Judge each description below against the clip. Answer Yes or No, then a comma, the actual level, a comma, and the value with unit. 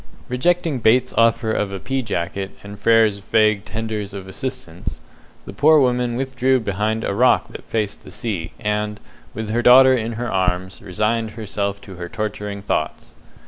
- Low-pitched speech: Yes, low, 110 Hz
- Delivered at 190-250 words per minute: No, average, 165 wpm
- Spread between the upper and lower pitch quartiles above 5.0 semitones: No, average, 3.4 semitones